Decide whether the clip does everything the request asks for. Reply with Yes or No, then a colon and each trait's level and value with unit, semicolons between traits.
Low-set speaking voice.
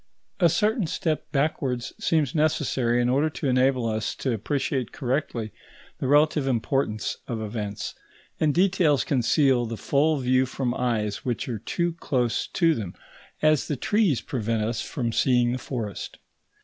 Yes: low, 130 Hz